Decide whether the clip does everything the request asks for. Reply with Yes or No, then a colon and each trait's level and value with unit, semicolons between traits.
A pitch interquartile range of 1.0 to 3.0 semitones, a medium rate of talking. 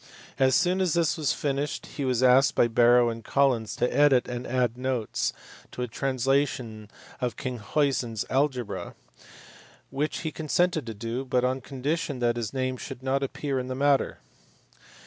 Yes: narrow, 2.5 semitones; average, 165 wpm